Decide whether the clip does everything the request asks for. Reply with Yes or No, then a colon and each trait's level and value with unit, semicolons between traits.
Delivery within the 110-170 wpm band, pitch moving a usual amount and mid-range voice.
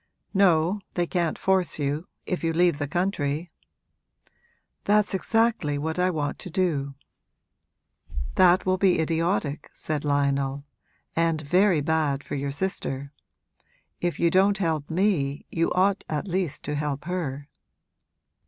Yes: slow, 135 wpm; average, 4.3 semitones; medium, 165 Hz